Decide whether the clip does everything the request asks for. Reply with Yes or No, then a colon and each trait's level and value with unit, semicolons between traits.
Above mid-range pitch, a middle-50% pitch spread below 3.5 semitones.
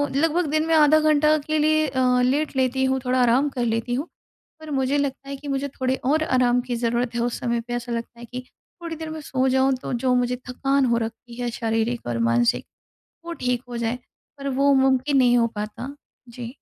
Yes: very high, 255 Hz; average, 2.9 semitones